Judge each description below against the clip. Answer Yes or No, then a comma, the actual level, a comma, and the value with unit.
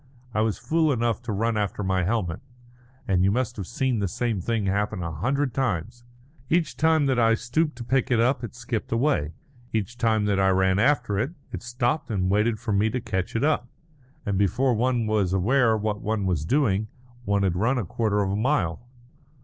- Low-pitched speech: Yes, low, 110 Hz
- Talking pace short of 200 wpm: No, fast, 205 wpm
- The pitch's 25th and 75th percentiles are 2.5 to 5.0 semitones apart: Yes, average, 4.0 semitones